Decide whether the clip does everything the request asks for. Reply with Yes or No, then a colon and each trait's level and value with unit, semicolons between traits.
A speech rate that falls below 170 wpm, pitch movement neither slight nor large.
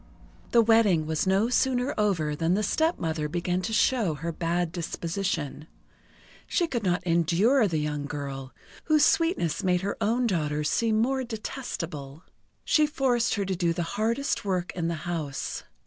No: average, 160 wpm; wide, 6.1 semitones